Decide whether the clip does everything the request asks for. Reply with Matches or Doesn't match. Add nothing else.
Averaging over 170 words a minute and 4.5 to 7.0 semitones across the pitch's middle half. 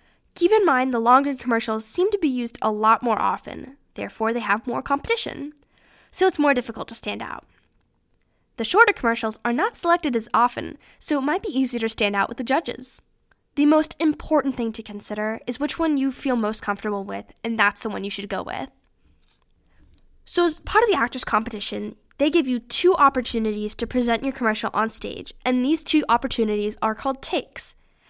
Matches